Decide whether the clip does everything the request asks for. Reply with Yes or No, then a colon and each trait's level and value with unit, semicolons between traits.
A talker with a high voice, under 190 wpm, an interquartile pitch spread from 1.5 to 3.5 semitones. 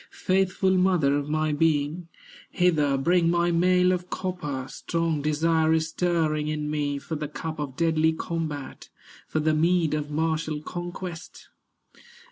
No: medium, 160 Hz; average, 140 wpm; narrow, 2.5 semitones